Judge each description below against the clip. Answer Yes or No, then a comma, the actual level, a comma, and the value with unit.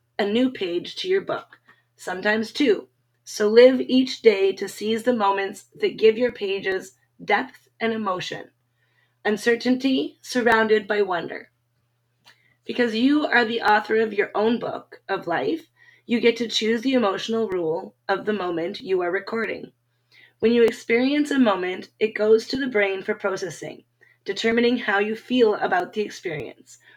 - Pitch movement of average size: Yes, average, 3.8 semitones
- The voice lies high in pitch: Yes, high, 215 Hz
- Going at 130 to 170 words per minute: Yes, average, 155 wpm